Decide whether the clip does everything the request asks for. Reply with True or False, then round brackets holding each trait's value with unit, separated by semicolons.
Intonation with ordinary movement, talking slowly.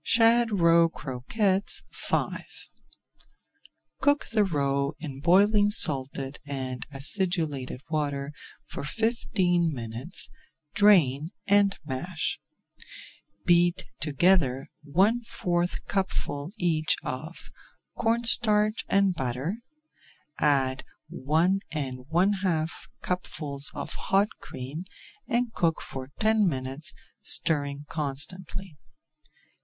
False (5.8 semitones; 95 wpm)